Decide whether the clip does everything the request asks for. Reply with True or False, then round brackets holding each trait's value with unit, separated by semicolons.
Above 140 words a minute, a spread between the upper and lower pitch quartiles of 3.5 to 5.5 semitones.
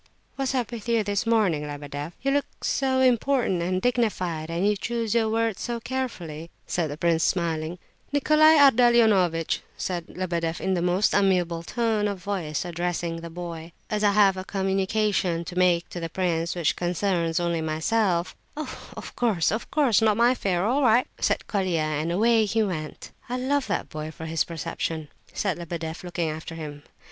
True (175 wpm; 5.2 semitones)